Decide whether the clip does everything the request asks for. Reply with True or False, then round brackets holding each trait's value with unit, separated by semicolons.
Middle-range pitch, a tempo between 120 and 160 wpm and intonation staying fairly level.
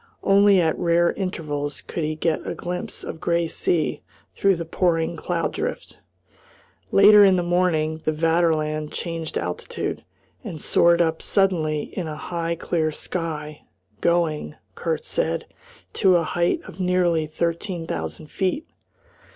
True (170 Hz; 140 wpm; 2.2 semitones)